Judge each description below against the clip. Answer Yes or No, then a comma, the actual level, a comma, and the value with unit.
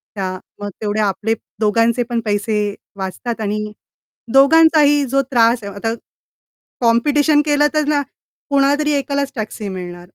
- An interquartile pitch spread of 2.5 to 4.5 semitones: No, wide, 5.5 semitones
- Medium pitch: No, high, 230 Hz